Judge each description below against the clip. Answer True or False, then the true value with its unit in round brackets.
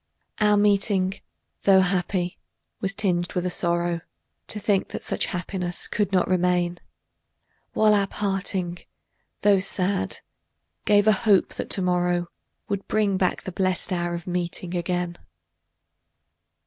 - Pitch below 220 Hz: True (185 Hz)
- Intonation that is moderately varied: False (2.2 semitones)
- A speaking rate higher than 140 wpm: False (135 wpm)